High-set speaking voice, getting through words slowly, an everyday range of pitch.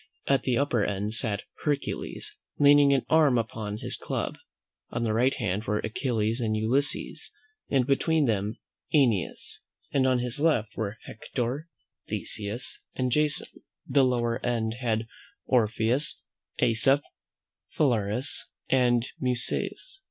No: low, 120 Hz; slow, 120 wpm; average, 3.8 semitones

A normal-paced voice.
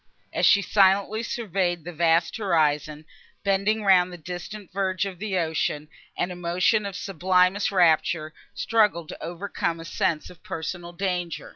Yes: average, 145 wpm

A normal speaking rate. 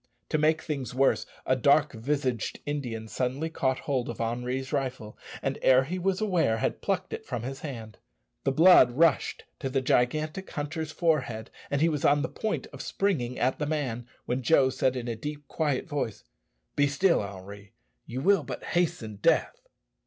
Yes: average, 180 wpm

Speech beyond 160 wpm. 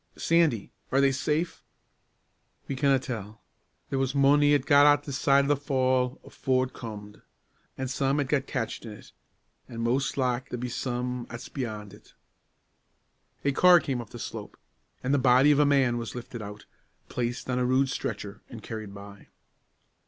Yes: average, 175 wpm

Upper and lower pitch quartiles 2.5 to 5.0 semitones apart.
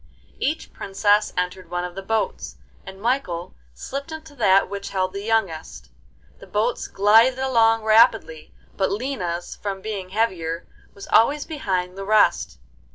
Yes: average, 3.6 semitones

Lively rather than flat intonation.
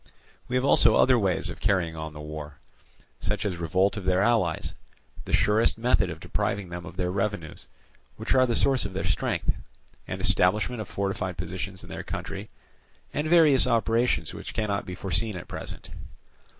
No: average, 4.2 semitones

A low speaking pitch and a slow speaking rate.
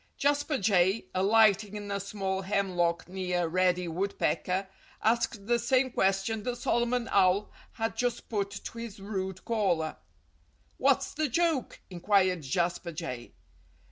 No: high, 200 Hz; slow, 130 wpm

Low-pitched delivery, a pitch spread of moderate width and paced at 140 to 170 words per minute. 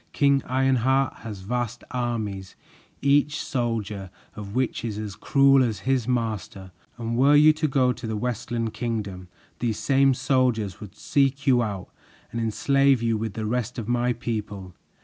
Yes: low, 120 Hz; average, 3.7 semitones; average, 160 wpm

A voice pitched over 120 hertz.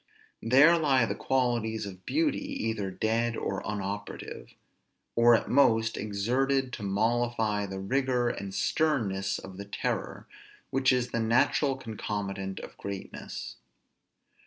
No: low, 115 Hz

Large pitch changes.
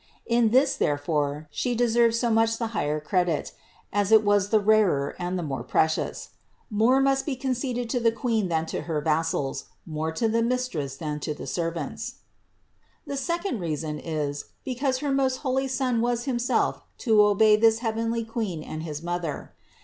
Yes: wide, 7.2 semitones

